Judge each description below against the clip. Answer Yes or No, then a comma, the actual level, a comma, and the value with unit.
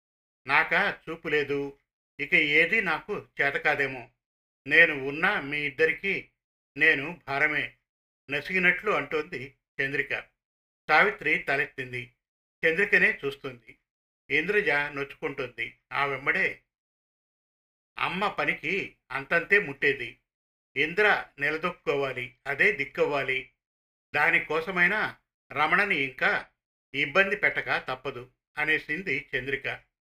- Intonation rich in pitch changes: No, average, 3.9 semitones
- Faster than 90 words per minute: No, average, 80 wpm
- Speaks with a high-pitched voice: No, medium, 140 Hz